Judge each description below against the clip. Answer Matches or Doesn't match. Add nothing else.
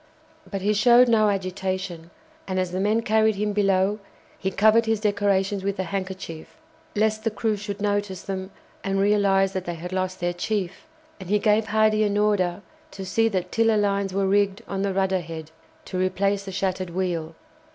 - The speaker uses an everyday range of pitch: Doesn't match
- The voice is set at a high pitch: Matches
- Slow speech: Doesn't match